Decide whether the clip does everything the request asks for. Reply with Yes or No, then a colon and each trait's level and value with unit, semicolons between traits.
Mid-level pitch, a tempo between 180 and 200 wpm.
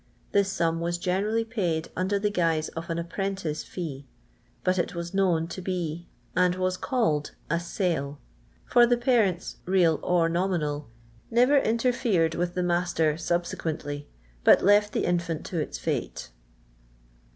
No: medium, 175 Hz; average, 150 wpm